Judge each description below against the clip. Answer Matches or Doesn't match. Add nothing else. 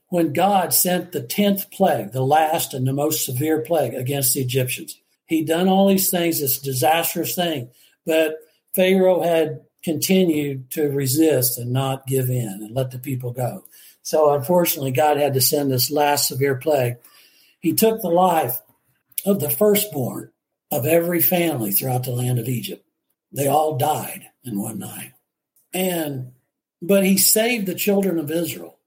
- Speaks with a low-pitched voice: Doesn't match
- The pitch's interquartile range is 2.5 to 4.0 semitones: Doesn't match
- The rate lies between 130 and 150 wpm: Doesn't match